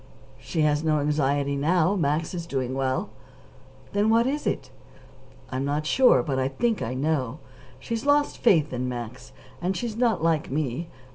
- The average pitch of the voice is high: No, medium, 155 Hz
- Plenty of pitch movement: Yes, wide, 6.2 semitones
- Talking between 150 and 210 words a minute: Yes, average, 170 wpm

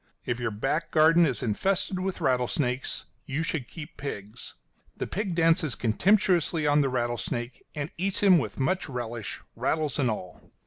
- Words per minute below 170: Yes, average, 160 wpm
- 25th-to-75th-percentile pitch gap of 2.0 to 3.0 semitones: No, wide, 5.6 semitones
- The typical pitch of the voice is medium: Yes, medium, 145 Hz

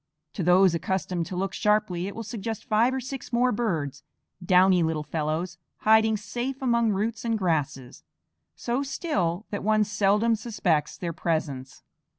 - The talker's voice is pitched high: Yes, high, 200 Hz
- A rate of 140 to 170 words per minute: Yes, average, 155 wpm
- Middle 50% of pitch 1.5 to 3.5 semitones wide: No, average, 4.9 semitones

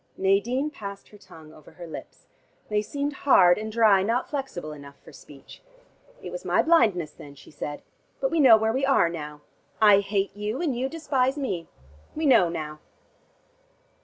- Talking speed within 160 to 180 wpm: Yes, average, 175 wpm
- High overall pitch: Yes, high, 210 Hz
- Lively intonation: Yes, wide, 7.7 semitones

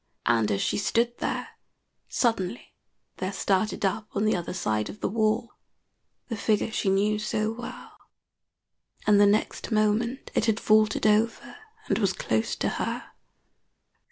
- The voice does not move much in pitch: Yes, narrow, 2.3 semitones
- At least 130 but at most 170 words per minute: Yes, average, 150 wpm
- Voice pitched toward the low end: No, high, 215 Hz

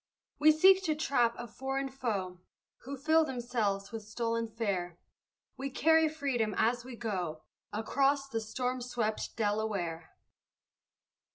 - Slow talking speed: Yes, slow, 125 wpm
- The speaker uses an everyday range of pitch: Yes, average, 4.3 semitones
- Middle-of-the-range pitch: No, high, 235 Hz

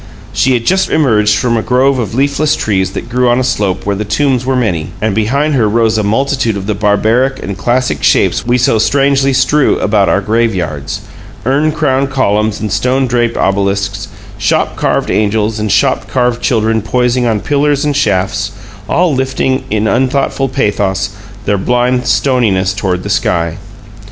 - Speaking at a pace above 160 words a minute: Yes, average, 170 wpm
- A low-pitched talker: Yes, low, 115 Hz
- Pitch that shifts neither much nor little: Yes, average, 4.3 semitones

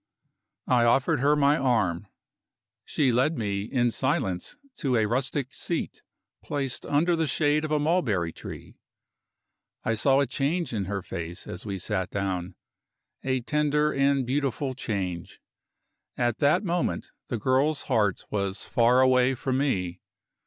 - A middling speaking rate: Yes, average, 145 wpm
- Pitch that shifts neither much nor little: No, wide, 5.9 semitones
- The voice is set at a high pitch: No, low, 130 Hz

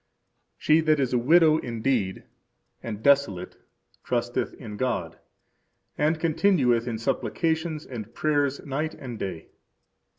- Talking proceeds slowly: Yes, slow, 120 wpm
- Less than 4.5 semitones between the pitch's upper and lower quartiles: No, average, 5.2 semitones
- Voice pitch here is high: No, low, 135 Hz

